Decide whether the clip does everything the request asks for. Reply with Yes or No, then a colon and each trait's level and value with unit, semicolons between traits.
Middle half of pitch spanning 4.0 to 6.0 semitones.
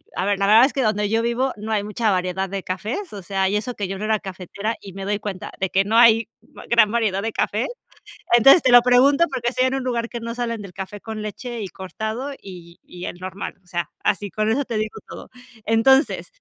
No: average, 3.3 semitones